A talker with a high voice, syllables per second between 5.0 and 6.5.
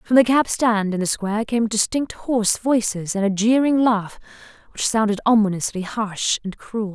No: high, 220 Hz; 4.8 syllables/s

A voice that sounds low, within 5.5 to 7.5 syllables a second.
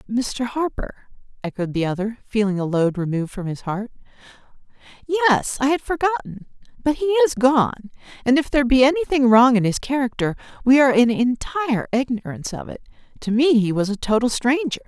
No: high, 245 Hz; 5.6 syllables/s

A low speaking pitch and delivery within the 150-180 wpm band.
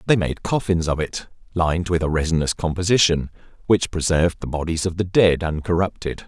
Yes: very low, 85 Hz; average, 170 wpm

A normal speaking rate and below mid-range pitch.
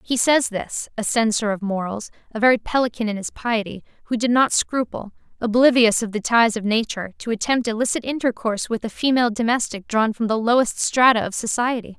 No: average, 190 wpm; high, 225 Hz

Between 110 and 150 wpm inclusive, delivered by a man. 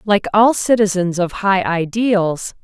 No: slow, 135 wpm; female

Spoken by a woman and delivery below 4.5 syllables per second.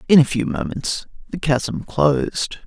No: male; 4.0 syllables/s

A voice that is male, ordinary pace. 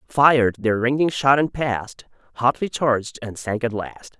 Yes: male; average, 170 wpm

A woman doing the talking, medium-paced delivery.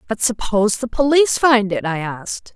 Yes: female; average, 190 wpm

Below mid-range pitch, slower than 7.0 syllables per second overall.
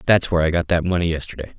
No: very low, 85 Hz; 7.9 syllables/s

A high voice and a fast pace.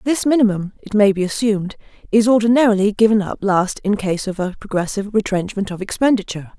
No: high, 205 Hz; average, 175 wpm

